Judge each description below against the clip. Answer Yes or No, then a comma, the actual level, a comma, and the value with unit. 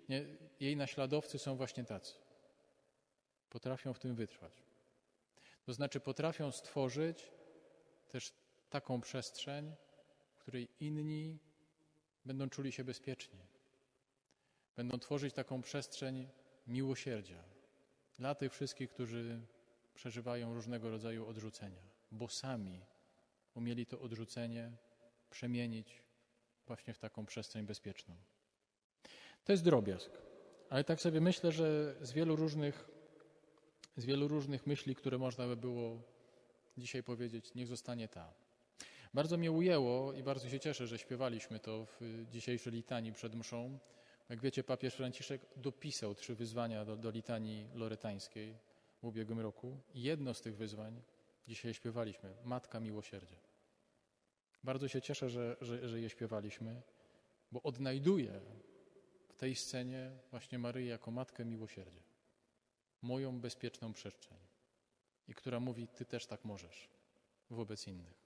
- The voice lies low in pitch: Yes, low, 125 Hz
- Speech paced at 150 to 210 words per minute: No, average, 120 wpm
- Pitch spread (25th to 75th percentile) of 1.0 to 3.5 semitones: Yes, average, 2.9 semitones